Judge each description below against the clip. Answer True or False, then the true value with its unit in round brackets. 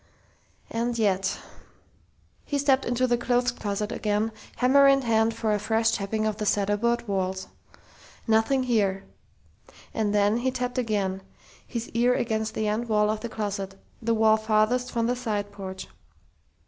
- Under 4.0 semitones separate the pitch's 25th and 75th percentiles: True (2.6 semitones)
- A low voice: False (220 Hz)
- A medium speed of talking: True (160 wpm)